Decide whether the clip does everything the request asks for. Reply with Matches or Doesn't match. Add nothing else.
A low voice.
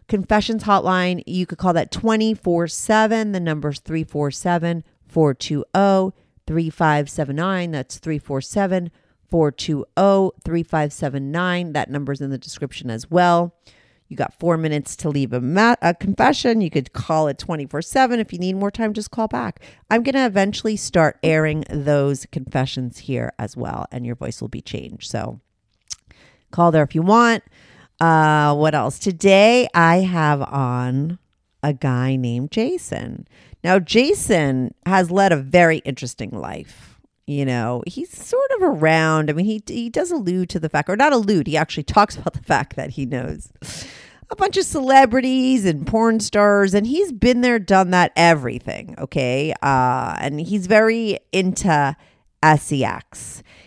Doesn't match